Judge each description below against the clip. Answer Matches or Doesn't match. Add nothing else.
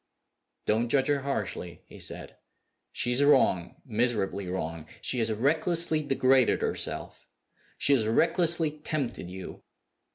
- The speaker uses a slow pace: Matches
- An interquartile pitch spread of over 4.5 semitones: Matches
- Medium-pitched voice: Doesn't match